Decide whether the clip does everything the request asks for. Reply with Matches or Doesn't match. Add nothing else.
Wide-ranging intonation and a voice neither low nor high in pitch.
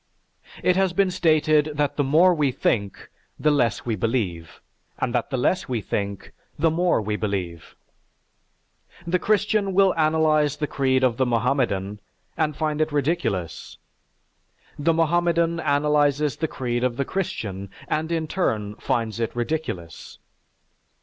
Matches